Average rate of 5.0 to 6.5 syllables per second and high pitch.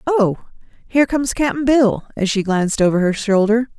Yes: 5.1 syllables/s; high, 225 Hz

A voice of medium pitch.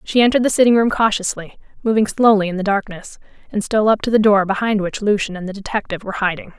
No: high, 205 Hz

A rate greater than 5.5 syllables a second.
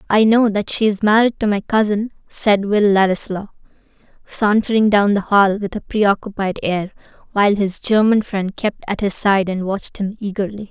No: 5.0 syllables/s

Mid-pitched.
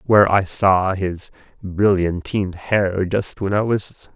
No: very low, 95 Hz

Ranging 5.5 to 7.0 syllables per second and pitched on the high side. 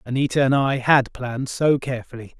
No: 5.8 syllables/s; low, 130 Hz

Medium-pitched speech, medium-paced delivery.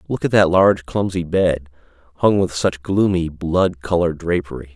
No: very low, 90 Hz; average, 165 wpm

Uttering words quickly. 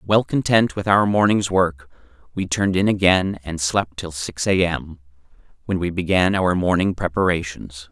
No: average, 165 wpm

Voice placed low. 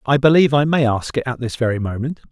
Yes: low, 130 Hz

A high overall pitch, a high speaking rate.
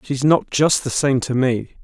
No: low, 135 Hz; fast, 230 wpm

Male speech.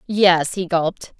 No: female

